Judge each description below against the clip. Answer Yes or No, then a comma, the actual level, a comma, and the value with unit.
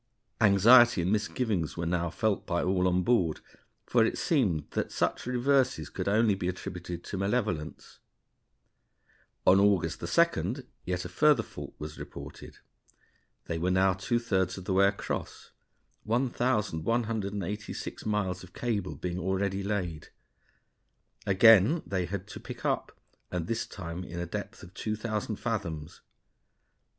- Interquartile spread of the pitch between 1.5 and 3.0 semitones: No, average, 3.9 semitones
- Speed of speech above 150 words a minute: No, average, 140 wpm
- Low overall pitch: Yes, very low, 95 Hz